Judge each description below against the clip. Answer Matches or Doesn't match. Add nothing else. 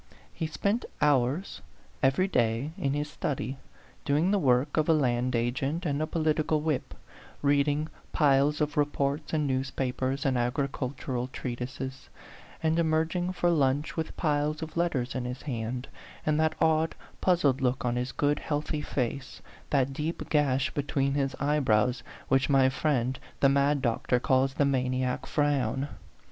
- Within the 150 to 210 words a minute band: Matches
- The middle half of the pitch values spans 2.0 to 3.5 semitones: Matches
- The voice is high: Doesn't match